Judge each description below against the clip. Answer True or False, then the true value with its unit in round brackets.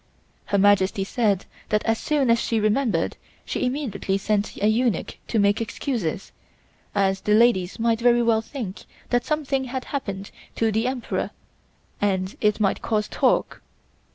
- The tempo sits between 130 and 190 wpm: True (155 wpm)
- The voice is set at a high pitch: True (220 Hz)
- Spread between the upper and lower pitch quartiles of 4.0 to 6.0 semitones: False (3.4 semitones)